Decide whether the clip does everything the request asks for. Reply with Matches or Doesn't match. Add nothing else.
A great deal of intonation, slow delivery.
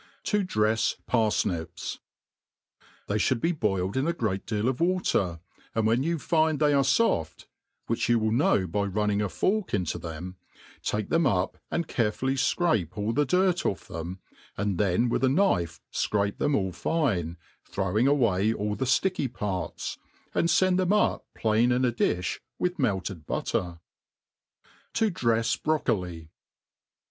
Doesn't match